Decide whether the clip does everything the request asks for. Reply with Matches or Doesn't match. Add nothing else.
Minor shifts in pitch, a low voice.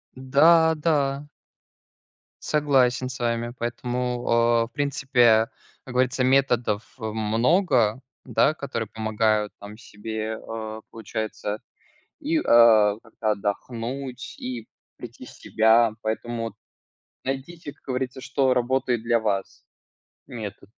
Doesn't match